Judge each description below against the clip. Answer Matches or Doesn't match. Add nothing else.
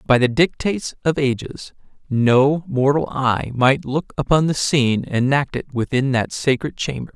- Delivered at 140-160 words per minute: Matches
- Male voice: Matches